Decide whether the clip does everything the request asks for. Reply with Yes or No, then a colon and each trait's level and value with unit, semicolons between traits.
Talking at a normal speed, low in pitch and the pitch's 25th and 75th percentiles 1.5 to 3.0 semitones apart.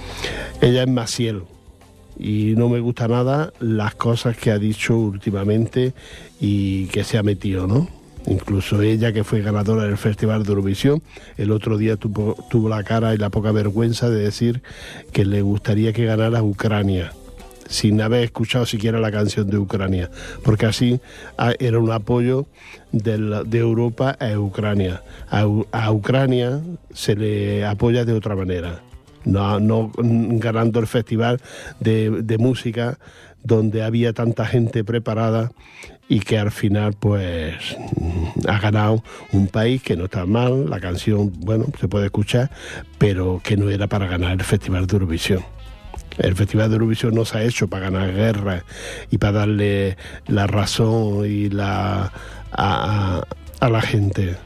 Yes: average, 155 wpm; low, 110 Hz; narrow, 2.4 semitones